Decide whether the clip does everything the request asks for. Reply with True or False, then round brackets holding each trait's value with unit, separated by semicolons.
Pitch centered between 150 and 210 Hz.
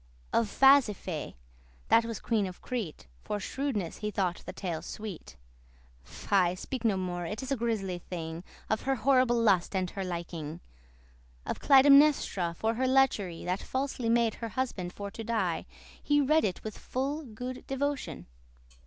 False (220 Hz)